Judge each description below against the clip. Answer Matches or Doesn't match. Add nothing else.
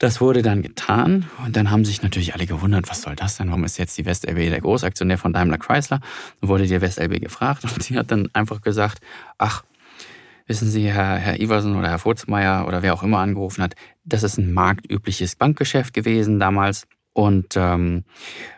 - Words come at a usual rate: Doesn't match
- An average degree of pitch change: Matches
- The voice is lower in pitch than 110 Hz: Matches